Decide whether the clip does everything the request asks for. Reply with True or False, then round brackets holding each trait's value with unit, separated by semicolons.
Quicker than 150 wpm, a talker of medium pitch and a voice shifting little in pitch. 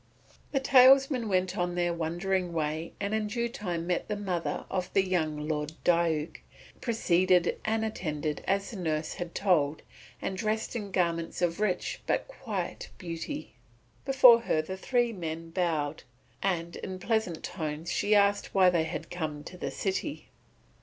False (160 wpm; 180 Hz; 4.1 semitones)